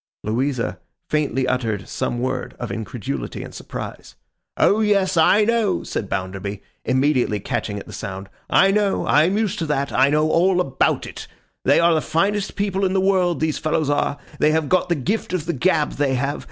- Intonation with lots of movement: Yes, wide, 6.7 semitones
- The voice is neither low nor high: Yes, medium, 150 Hz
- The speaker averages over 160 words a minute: Yes, average, 195 wpm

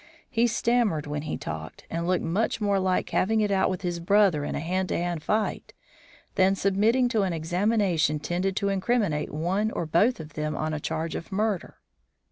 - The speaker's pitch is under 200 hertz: Yes, medium, 185 Hz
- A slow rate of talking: No, average, 195 wpm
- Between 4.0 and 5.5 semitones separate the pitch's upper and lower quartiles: Yes, average, 4.4 semitones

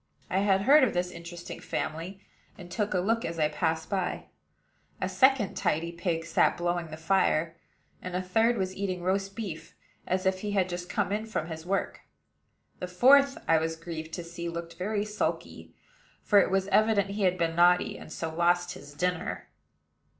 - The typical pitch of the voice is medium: Yes, medium, 180 Hz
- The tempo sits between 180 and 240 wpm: Yes, average, 185 wpm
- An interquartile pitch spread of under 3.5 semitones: Yes, average, 2.9 semitones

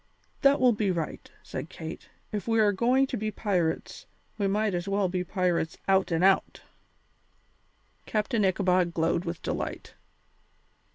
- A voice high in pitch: Yes, high, 195 Hz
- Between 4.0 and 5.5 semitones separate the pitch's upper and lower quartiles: No, average, 3.2 semitones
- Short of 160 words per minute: Yes, average, 145 wpm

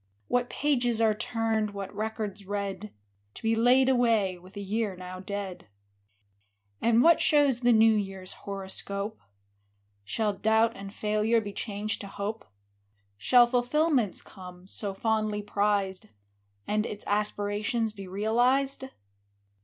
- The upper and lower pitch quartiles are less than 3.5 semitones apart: Yes, narrow, 2.5 semitones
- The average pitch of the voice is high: Yes, high, 210 Hz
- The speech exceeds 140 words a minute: No, slow, 135 wpm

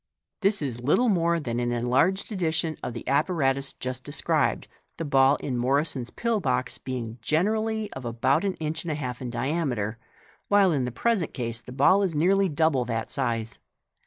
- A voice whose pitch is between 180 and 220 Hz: No, medium, 140 Hz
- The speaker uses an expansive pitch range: Yes, wide, 5.7 semitones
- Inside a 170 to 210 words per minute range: Yes, average, 185 wpm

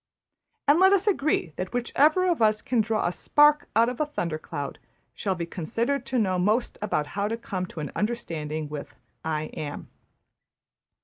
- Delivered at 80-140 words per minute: No, average, 175 wpm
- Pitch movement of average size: No, wide, 8.1 semitones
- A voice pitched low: No, high, 215 Hz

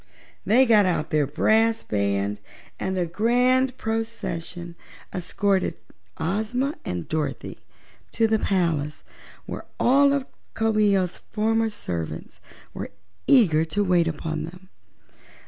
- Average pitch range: No, wide, 5.7 semitones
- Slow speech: Yes, slow, 120 wpm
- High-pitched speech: Yes, high, 195 Hz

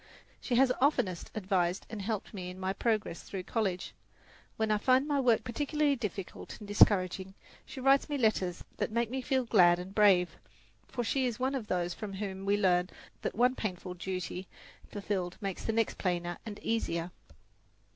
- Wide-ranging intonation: No, average, 4.6 semitones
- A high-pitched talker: Yes, high, 205 Hz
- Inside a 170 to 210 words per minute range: Yes, average, 175 wpm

